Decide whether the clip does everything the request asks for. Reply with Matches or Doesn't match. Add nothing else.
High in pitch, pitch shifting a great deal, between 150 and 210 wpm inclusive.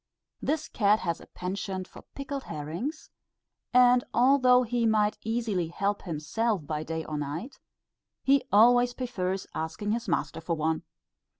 Doesn't match